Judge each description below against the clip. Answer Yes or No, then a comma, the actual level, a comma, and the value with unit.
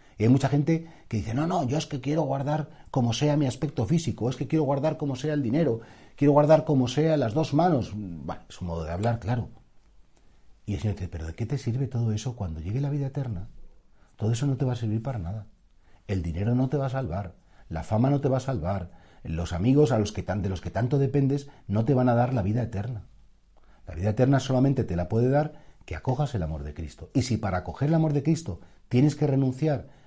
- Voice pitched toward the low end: Yes, low, 120 Hz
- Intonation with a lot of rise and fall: Yes, wide, 6.4 semitones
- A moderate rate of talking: No, fast, 245 wpm